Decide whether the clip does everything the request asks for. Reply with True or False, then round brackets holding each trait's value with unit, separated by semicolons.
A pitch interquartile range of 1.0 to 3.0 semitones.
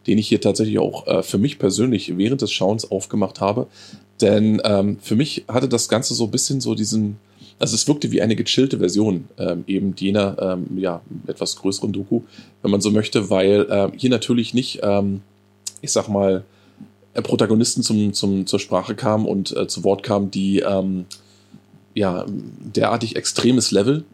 True (2.5 semitones)